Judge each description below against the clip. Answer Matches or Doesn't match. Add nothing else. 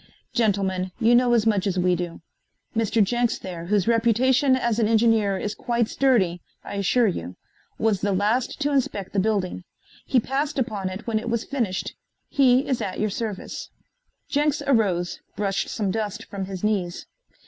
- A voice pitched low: Doesn't match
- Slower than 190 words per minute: Matches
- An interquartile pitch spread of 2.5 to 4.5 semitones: Matches